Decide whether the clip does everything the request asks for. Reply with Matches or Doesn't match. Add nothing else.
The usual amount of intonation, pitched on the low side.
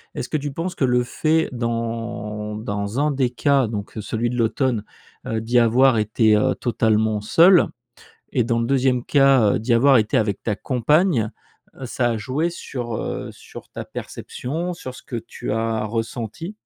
Matches